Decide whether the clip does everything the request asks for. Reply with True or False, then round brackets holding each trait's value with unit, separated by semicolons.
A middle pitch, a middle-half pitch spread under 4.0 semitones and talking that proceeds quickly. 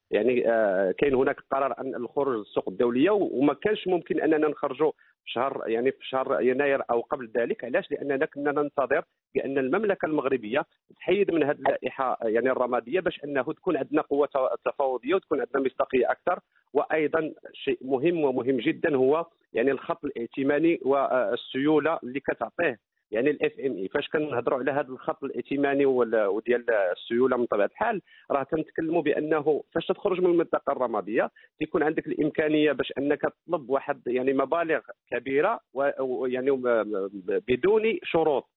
False (150 Hz; 3.6 semitones; 140 wpm)